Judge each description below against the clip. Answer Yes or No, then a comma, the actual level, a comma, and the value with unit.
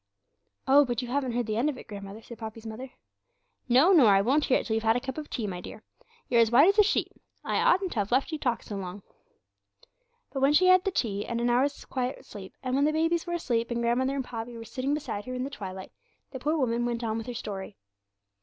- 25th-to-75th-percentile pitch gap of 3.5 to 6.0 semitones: Yes, average, 4.0 semitones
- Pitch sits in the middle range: No, high, 245 Hz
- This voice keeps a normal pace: No, fast, 260 wpm